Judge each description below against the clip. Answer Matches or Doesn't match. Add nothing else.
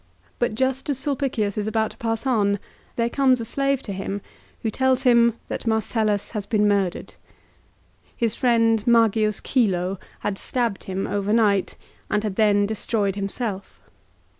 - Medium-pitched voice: Doesn't match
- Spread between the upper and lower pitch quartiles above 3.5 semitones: Doesn't match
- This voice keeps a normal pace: Matches